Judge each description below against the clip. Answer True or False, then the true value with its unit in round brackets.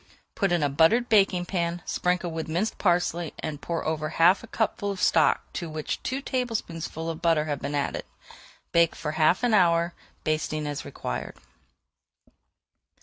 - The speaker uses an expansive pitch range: False (3.2 semitones)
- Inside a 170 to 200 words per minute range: False (160 wpm)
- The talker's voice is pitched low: False (170 Hz)